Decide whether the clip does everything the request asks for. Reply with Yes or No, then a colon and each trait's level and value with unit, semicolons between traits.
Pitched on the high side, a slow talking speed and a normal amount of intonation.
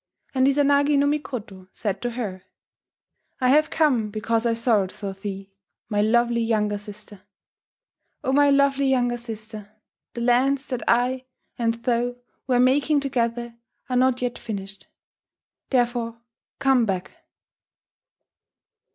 Yes: high, 240 Hz; slow, 125 wpm; average, 3.4 semitones